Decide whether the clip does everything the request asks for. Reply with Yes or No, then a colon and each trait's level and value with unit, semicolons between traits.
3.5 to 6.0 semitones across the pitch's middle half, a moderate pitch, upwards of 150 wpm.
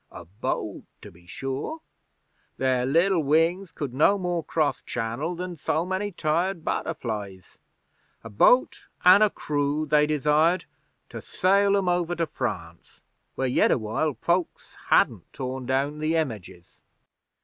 No: wide, 5.4 semitones; medium, 155 Hz; average, 140 wpm